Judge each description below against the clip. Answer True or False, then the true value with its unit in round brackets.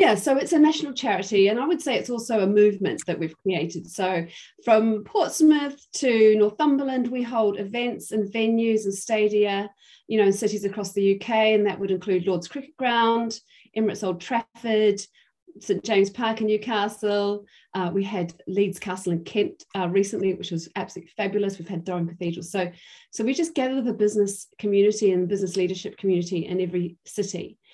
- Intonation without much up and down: False (3.2 semitones)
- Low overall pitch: False (205 Hz)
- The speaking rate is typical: True (180 wpm)